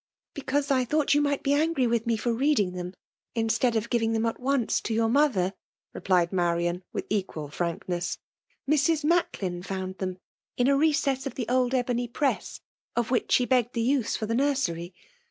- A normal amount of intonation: No, wide, 6.4 semitones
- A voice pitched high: Yes, high, 235 Hz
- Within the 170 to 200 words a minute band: Yes, average, 190 wpm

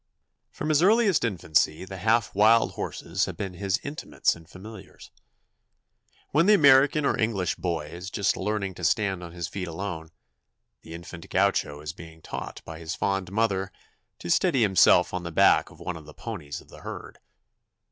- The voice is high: No, very low, 95 Hz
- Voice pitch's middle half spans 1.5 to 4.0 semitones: No, average, 5.0 semitones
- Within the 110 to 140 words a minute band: No, average, 175 wpm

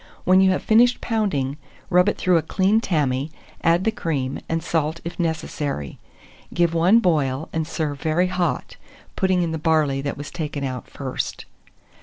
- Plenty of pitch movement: No, average, 4.1 semitones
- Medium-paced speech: Yes, average, 170 wpm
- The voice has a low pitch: No, medium, 165 Hz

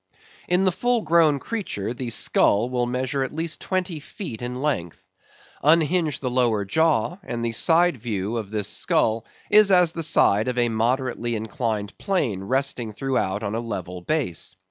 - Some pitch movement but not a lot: No, wide, 6.5 semitones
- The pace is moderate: Yes, average, 165 wpm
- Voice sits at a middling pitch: No, low, 125 Hz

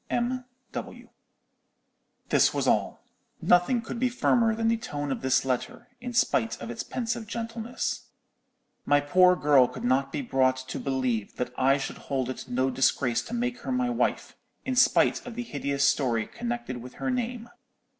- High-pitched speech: No, medium, 150 Hz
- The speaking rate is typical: Yes, average, 175 wpm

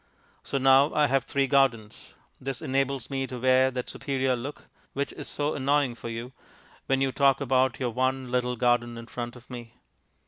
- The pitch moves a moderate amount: No, narrow, 1.9 semitones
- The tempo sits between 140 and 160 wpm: No, average, 185 wpm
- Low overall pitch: Yes, low, 130 Hz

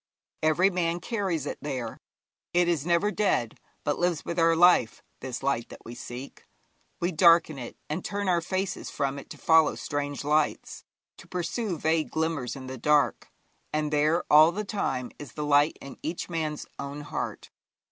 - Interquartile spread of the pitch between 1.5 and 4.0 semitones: Yes, average, 3.4 semitones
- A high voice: No, medium, 155 Hz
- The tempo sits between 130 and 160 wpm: No, average, 175 wpm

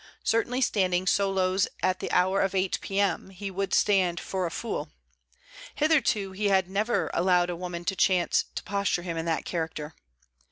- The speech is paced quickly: No, average, 170 wpm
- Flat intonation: Yes, narrow, 1.9 semitones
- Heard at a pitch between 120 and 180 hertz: No, high, 190 Hz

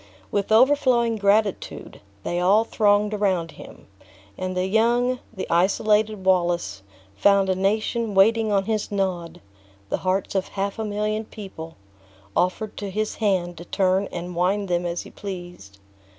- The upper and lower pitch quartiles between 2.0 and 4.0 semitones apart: Yes, average, 2.9 semitones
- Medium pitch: No, high, 200 Hz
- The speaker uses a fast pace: No, average, 150 wpm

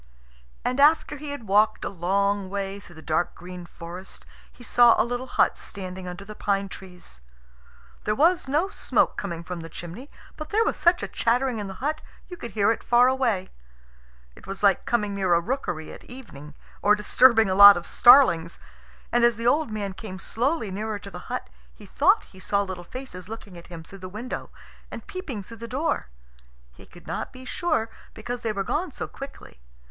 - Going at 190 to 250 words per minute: Yes, average, 200 wpm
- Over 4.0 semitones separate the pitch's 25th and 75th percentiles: Yes, average, 5.2 semitones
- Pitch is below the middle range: No, high, 210 Hz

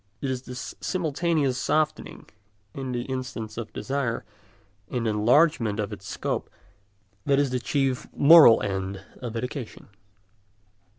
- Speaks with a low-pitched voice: Yes, low, 125 Hz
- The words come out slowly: Yes, slow, 125 wpm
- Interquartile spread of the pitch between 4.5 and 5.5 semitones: No, average, 3.6 semitones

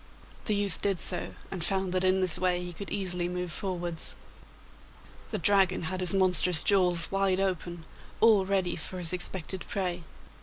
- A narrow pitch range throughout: Yes, narrow, 1.5 semitones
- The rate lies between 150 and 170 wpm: Yes, average, 165 wpm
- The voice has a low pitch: No, medium, 185 Hz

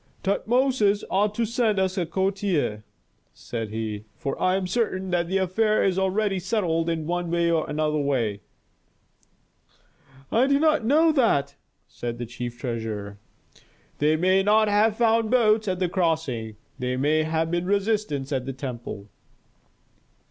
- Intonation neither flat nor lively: No, wide, 7.3 semitones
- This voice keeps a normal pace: Yes, average, 150 wpm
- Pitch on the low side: No, medium, 180 Hz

